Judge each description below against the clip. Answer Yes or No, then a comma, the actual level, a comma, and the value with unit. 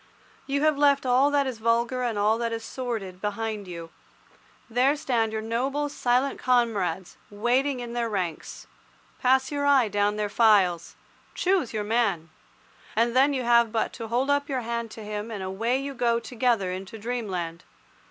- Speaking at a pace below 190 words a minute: Yes, average, 170 wpm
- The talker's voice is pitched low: No, high, 235 Hz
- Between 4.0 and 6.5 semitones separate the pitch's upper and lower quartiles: No, average, 3.6 semitones